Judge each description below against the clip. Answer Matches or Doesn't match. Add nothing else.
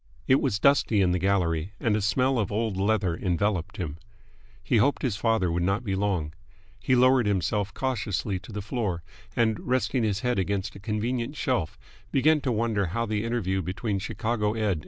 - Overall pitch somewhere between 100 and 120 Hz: Matches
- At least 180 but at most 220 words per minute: Matches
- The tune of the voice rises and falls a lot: Doesn't match